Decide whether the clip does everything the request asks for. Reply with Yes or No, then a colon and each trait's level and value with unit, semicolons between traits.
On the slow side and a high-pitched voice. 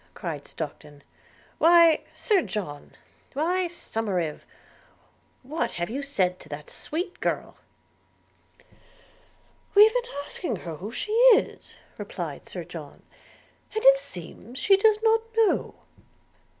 Yes: slow, 120 wpm; very high, 280 Hz